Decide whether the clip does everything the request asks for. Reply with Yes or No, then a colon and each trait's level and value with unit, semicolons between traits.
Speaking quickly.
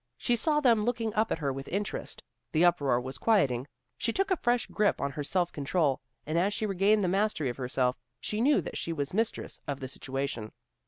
Yes: fast, 215 wpm